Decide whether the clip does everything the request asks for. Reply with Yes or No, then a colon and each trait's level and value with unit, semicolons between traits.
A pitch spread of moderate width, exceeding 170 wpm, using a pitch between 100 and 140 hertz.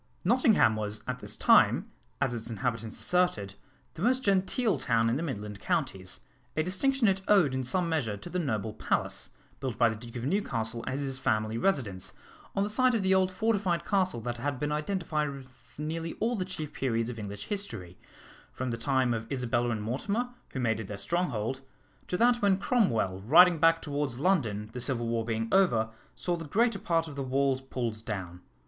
No: wide, 8.2 semitones; average, 195 wpm; low, 135 Hz